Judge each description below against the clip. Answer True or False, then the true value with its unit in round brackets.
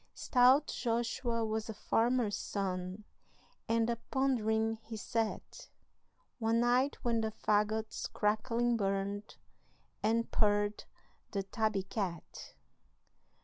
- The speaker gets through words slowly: True (105 wpm)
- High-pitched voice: True (220 Hz)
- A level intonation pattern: True (2.2 semitones)